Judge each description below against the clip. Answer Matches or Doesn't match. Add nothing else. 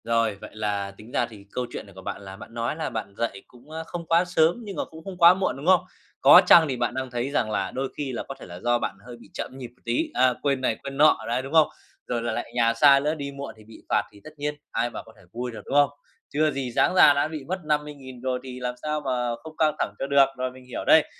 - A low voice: Matches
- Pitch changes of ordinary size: Matches